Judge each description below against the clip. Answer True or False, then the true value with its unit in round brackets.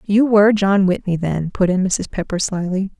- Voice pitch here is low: False (190 Hz)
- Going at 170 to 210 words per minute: True (200 wpm)